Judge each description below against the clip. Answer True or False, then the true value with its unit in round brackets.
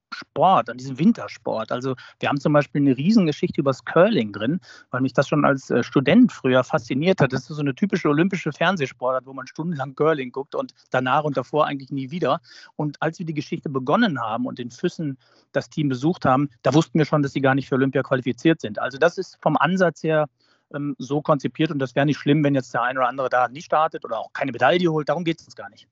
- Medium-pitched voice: True (145 Hz)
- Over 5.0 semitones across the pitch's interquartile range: False (3.2 semitones)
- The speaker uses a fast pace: True (240 wpm)